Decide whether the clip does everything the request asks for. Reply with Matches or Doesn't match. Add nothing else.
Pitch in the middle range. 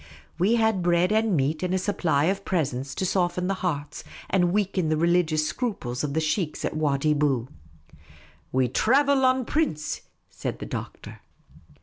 Matches